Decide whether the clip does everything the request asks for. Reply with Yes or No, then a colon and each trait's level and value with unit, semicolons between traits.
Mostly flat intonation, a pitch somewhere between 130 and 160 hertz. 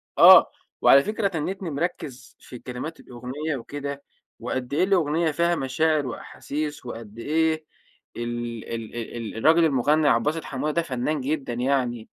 No: average, 4.5 semitones; medium, 140 Hz